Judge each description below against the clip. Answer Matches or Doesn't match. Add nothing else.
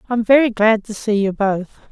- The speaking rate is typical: Doesn't match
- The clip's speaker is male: Doesn't match